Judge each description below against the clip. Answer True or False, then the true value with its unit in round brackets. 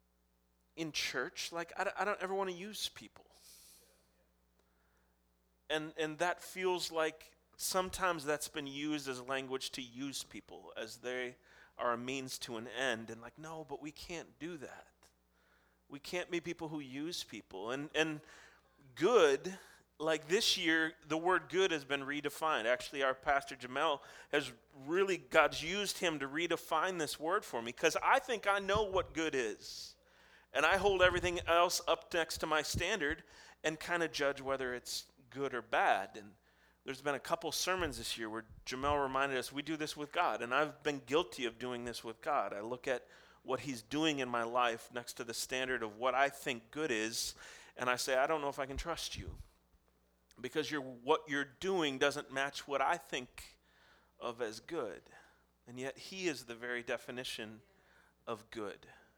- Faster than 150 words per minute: True (185 wpm)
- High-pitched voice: False (140 Hz)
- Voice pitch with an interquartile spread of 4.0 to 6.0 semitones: True (5.1 semitones)